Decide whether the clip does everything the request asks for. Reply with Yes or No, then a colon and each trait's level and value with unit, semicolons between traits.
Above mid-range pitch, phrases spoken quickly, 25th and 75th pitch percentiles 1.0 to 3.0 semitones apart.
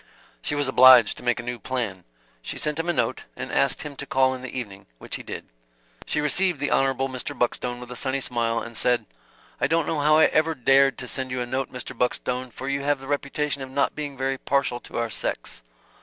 No: low, 130 Hz; fast, 235 wpm; narrow, 2.5 semitones